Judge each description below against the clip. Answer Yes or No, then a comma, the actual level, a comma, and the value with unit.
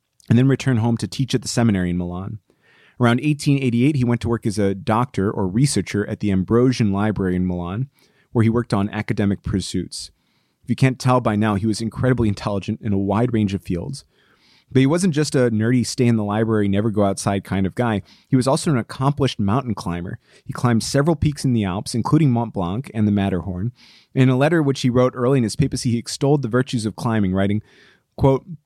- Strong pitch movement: No, average, 4.2 semitones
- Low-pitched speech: Yes, low, 115 Hz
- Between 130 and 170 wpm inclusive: No, fast, 205 wpm